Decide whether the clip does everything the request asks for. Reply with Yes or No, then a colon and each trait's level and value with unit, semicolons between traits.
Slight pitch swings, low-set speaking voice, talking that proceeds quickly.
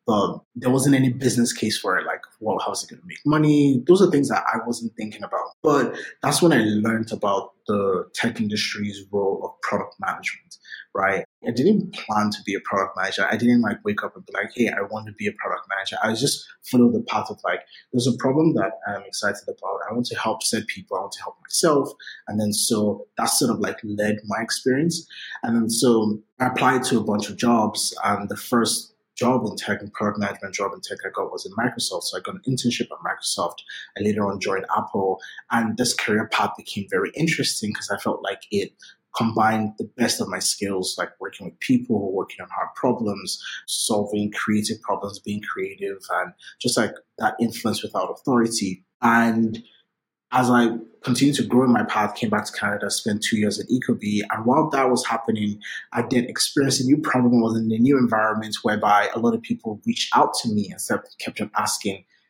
No: average, 4.2 semitones; low, 115 Hz; fast, 215 wpm